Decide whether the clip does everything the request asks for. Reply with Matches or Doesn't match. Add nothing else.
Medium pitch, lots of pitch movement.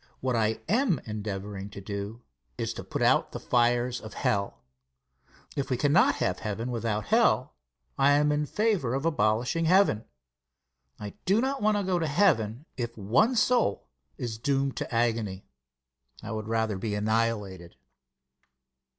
Doesn't match